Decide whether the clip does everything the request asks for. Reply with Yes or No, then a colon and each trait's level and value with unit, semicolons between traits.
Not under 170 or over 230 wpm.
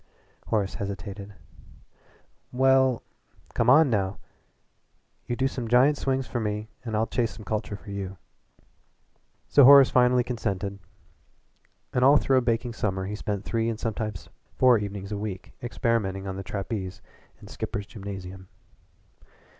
No: average, 145 wpm